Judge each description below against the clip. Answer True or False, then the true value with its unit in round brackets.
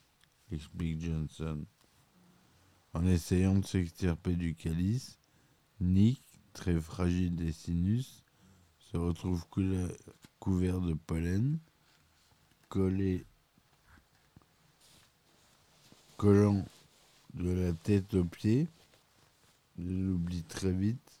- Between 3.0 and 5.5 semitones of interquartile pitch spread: False (2.4 semitones)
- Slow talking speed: True (80 wpm)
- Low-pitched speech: True (90 Hz)